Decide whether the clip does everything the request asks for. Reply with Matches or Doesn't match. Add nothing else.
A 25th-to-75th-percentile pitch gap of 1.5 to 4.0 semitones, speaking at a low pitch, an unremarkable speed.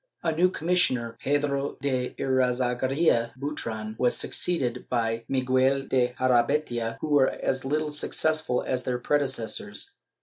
Doesn't match